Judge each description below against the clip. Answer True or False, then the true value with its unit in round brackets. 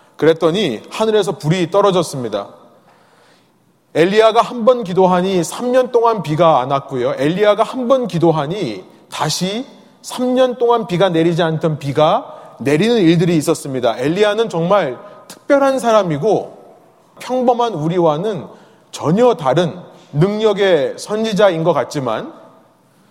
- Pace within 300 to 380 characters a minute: False (275 characters per minute)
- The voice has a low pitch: False (195 Hz)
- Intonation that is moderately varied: False (5.9 semitones)